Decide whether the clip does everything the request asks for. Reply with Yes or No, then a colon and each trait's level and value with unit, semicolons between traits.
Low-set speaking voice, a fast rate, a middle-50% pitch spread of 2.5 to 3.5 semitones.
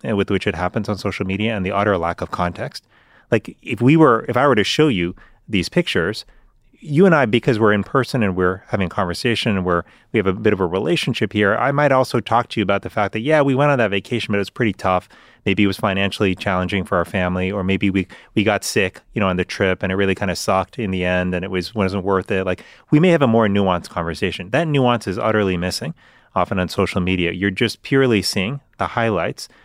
No: low, 100 Hz; fast, 255 wpm; average, 4.2 semitones